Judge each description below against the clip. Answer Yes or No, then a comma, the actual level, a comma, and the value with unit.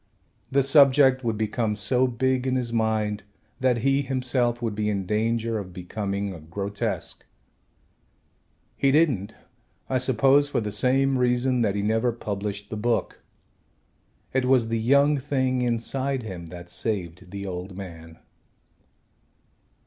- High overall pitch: No, low, 115 Hz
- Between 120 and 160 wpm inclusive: Yes, average, 140 wpm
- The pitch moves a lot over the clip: No, average, 4.2 semitones